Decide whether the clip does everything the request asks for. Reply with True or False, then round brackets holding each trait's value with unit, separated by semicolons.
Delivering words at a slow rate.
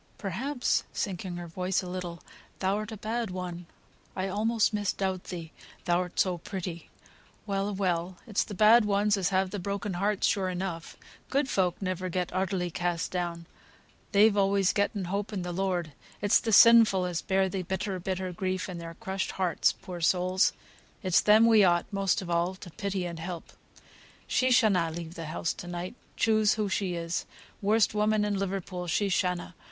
False (180 wpm)